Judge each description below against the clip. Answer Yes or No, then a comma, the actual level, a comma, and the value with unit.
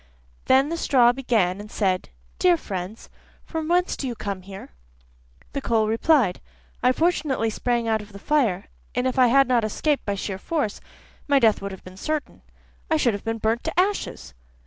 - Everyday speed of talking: Yes, average, 190 wpm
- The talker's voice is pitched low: No, high, 235 Hz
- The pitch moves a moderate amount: No, wide, 5.9 semitones